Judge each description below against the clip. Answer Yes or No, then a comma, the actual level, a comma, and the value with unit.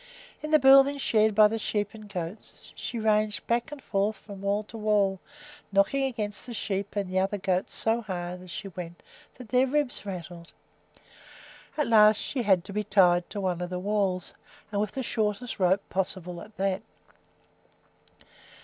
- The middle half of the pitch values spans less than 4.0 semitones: Yes, average, 2.9 semitones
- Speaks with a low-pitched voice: No, high, 205 Hz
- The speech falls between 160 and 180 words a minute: Yes, average, 175 wpm